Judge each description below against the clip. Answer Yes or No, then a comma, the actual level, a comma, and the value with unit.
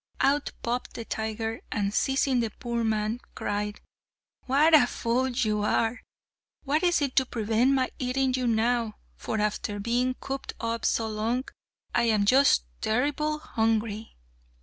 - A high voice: Yes, high, 235 Hz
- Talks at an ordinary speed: Yes, average, 145 wpm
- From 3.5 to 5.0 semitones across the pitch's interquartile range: No, average, 3.0 semitones